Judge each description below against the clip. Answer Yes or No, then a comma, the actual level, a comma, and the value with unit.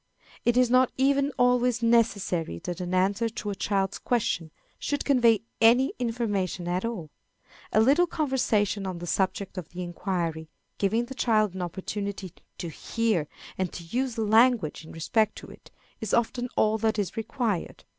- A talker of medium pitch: No, high, 215 Hz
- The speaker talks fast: No, average, 165 wpm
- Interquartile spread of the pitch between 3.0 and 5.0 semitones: Yes, average, 4.5 semitones